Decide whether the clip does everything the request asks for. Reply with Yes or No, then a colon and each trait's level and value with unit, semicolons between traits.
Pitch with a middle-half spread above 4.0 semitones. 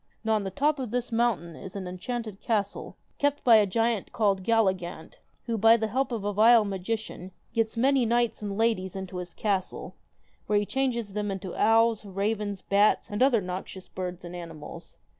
No: average, 3.3 semitones